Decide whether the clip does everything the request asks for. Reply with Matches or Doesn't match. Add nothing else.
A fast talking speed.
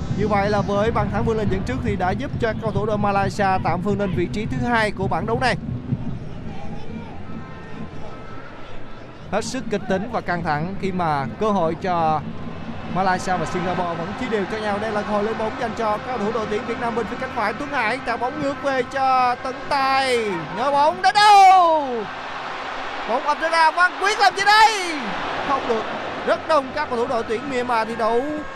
Doesn't match